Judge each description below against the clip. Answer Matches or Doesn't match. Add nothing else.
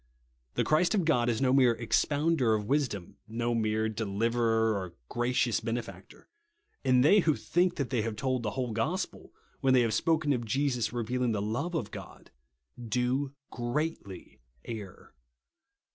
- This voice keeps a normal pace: Matches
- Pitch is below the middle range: Matches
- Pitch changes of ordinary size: Matches